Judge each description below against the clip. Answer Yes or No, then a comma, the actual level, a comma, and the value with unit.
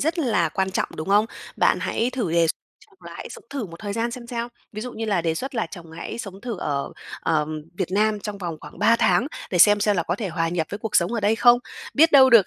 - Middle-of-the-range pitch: No, high, 205 Hz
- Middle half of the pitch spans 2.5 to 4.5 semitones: No, average, 5.3 semitones